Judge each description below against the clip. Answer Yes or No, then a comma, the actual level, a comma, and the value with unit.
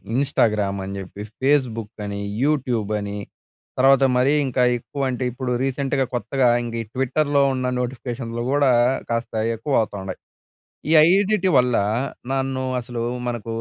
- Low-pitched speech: Yes, low, 125 Hz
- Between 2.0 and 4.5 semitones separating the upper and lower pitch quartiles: Yes, average, 2.8 semitones